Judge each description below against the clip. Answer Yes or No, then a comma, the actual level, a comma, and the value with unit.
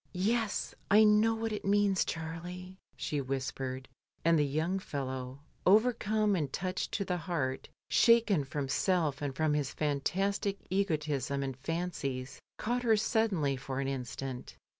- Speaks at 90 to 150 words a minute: Yes, average, 140 wpm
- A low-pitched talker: No, medium, 165 Hz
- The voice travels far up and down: Yes, wide, 6.6 semitones